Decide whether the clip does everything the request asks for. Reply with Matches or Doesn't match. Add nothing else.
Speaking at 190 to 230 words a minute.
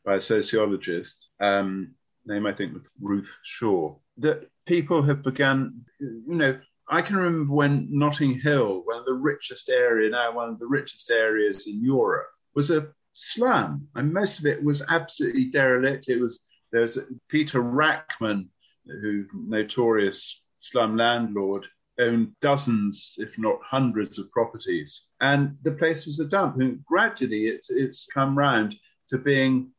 Doesn't match